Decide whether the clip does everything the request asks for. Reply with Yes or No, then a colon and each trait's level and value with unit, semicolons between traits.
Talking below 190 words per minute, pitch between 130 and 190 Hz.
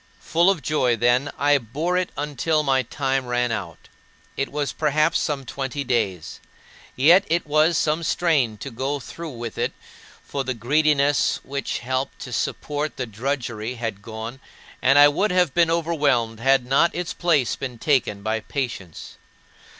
Yes: average, 160 wpm; low, 135 Hz